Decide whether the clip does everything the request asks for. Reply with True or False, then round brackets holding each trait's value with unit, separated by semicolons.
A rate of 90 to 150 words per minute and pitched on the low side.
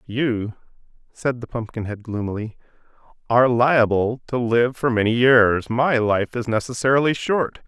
True (135 wpm; 120 Hz)